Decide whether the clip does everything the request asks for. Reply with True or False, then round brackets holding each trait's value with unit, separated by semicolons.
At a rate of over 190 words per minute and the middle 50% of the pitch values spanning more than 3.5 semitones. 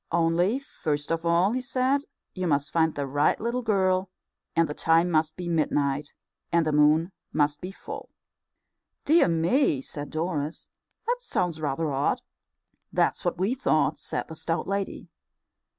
False (155 wpm; 4.0 semitones)